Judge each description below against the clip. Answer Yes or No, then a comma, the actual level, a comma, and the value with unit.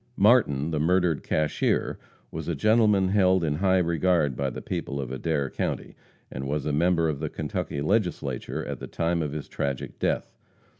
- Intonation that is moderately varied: Yes, average, 4.4 semitones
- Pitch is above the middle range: No, very low, 80 Hz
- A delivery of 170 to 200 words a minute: Yes, average, 180 wpm